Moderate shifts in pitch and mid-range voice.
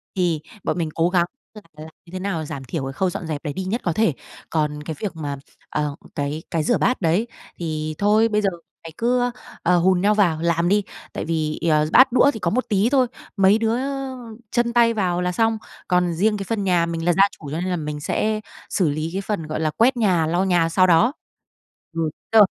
Yes: average, 4.8 semitones; medium, 180 Hz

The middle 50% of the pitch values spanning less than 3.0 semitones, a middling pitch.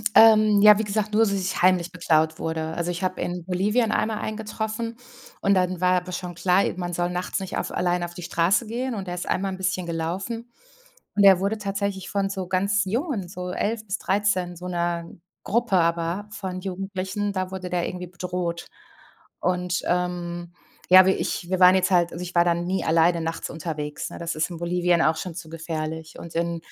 Yes: narrow, 2.4 semitones; medium, 180 Hz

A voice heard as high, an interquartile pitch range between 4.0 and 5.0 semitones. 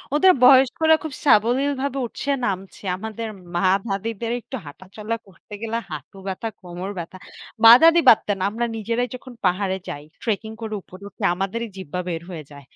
Yes: high, 215 Hz; average, 4.3 semitones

